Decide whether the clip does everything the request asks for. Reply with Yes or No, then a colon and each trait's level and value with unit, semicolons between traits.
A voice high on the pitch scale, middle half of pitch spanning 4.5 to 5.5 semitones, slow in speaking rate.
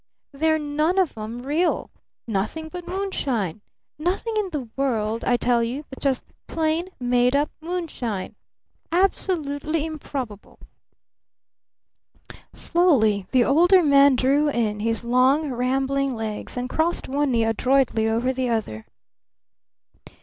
Yes: very high, 270 Hz; average, 5.1 semitones; slow, 120 wpm